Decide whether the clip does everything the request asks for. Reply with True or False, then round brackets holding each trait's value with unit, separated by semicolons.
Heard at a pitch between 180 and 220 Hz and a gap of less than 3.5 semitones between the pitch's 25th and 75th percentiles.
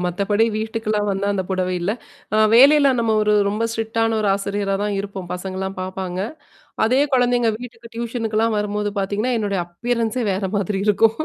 True (210 Hz; 2.6 semitones)